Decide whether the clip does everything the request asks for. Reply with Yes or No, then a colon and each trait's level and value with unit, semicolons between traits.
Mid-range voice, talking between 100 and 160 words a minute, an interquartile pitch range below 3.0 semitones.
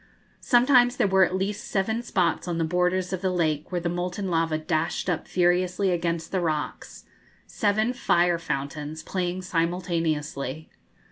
Yes: medium, 175 Hz; average, 150 wpm; narrow, 2.4 semitones